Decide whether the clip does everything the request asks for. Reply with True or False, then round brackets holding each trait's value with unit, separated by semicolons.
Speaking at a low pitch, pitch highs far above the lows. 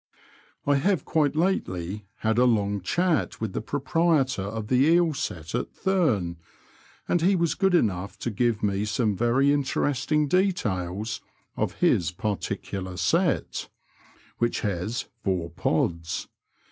True (115 Hz; 7.5 semitones)